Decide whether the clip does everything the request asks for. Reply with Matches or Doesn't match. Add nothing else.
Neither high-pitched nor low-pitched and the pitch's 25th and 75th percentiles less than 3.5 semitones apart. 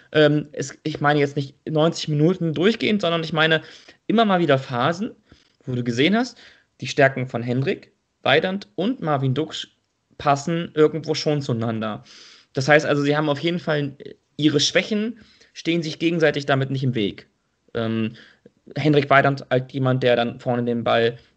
Doesn't match